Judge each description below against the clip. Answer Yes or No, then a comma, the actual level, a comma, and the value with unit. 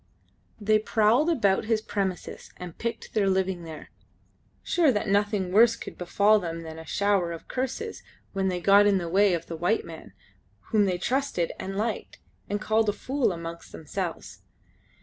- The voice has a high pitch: Yes, high, 200 Hz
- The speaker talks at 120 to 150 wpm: No, average, 170 wpm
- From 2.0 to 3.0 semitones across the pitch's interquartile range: No, average, 3.5 semitones